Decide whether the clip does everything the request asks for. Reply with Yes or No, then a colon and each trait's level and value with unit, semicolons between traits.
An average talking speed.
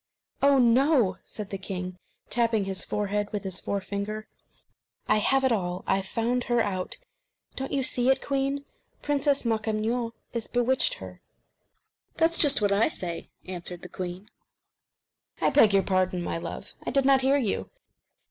Yes: average, 155 wpm